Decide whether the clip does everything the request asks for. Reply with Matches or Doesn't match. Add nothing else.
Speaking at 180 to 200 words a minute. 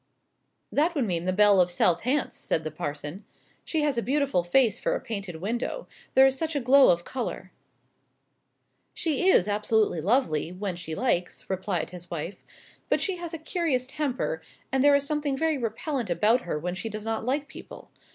Matches